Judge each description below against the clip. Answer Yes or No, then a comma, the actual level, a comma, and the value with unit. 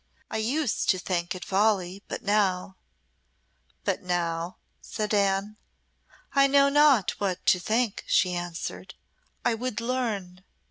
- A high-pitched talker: Yes, high, 200 Hz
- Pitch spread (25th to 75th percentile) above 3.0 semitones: Yes, average, 4.0 semitones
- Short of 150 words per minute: Yes, average, 140 wpm